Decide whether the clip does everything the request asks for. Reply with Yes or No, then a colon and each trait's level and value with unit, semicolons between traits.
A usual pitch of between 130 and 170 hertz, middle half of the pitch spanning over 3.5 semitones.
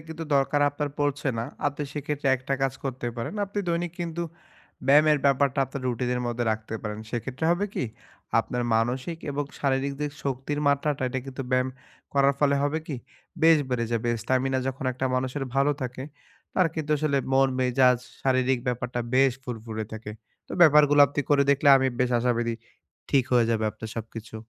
No: low, 135 Hz; average, 2.8 semitones